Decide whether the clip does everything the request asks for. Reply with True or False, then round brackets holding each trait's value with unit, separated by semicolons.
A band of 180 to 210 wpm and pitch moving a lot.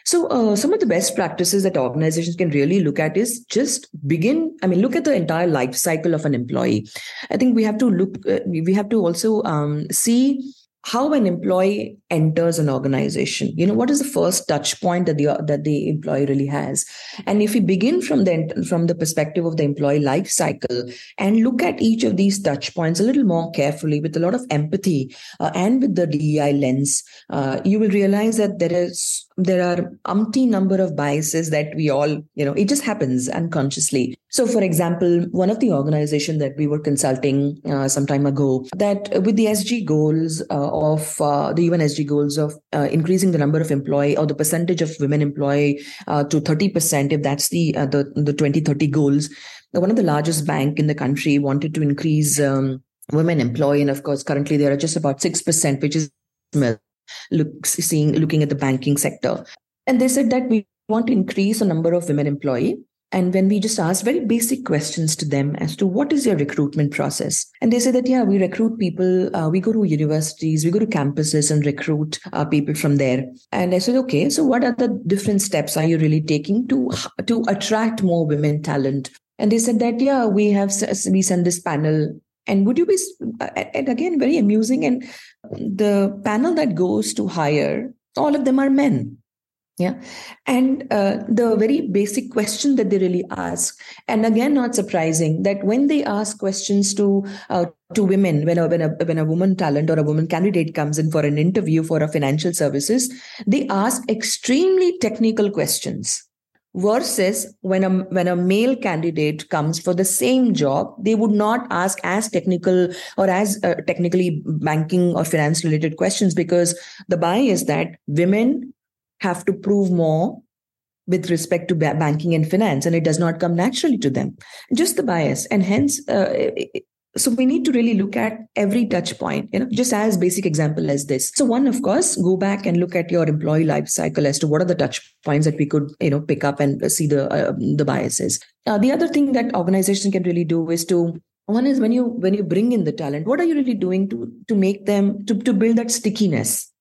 True (205 wpm; 6.2 semitones)